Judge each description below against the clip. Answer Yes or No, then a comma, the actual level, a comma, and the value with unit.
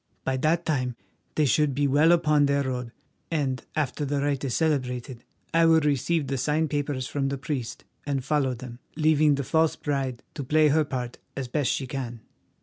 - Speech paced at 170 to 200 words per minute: Yes, average, 190 wpm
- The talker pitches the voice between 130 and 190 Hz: Yes, medium, 140 Hz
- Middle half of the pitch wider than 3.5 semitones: No, average, 2.8 semitones